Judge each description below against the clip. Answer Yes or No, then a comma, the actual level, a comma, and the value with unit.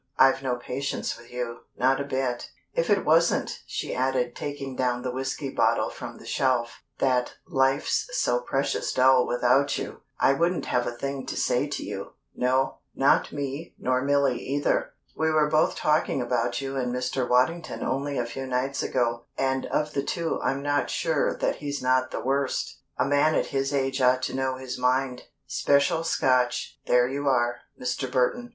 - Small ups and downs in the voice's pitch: Yes, narrow, 2.0 semitones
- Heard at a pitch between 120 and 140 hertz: Yes, low, 135 Hz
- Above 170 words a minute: Yes, average, 180 wpm